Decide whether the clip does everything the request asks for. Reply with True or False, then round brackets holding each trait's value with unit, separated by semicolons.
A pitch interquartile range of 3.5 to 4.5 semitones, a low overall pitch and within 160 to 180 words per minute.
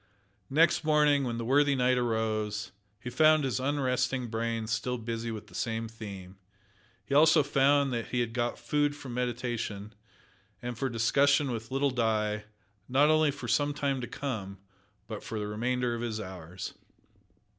True (3.8 semitones; 125 Hz; 165 wpm)